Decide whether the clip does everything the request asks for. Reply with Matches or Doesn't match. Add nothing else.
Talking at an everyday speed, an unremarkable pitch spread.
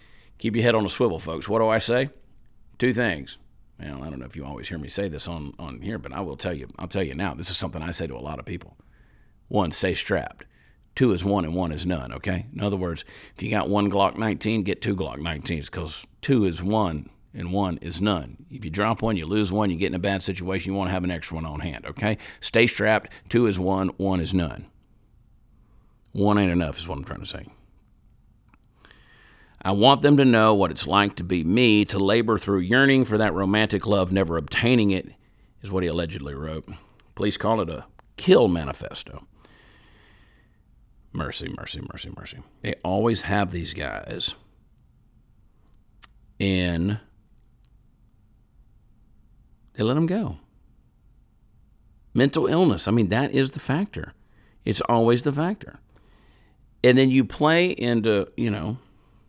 Matches